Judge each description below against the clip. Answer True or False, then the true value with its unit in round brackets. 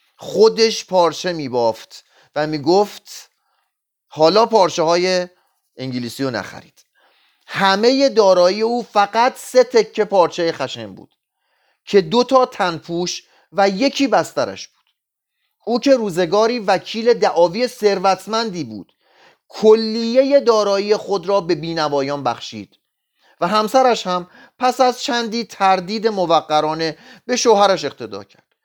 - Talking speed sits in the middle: True (115 wpm)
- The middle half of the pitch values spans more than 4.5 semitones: True (5.3 semitones)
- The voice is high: True (200 Hz)